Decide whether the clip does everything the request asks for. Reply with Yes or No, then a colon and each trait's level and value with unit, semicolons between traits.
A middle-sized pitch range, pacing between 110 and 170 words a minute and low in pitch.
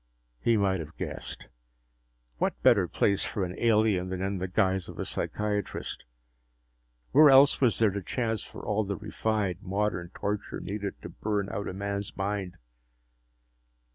No: narrow, 2.1 semitones; average, 155 wpm; low, 100 Hz